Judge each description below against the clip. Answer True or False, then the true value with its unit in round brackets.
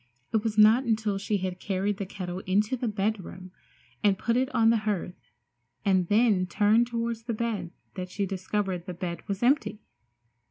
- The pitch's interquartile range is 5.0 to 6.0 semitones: False (3.2 semitones)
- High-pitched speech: True (205 Hz)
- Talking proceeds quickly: False (175 wpm)